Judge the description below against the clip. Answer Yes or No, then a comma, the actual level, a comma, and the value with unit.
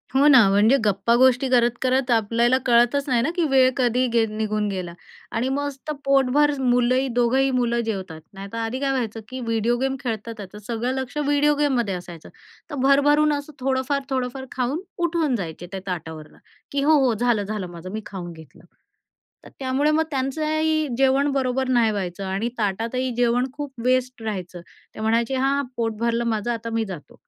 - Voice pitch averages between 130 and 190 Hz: No, high, 245 Hz